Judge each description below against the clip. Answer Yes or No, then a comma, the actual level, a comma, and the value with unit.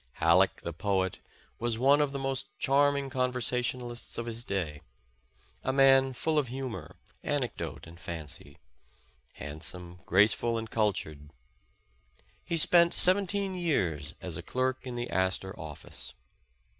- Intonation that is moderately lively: No, wide, 7.2 semitones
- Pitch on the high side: No, low, 120 Hz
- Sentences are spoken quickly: No, slow, 135 wpm